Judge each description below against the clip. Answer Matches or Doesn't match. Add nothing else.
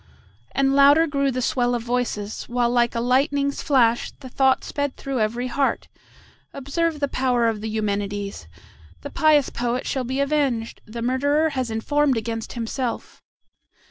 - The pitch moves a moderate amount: Matches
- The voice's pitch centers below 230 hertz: Doesn't match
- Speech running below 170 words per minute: Matches